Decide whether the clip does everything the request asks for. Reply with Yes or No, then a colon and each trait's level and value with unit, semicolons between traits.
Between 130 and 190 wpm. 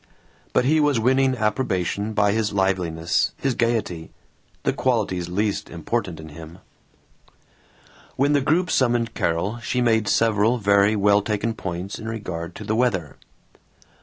Yes: average, 140 wpm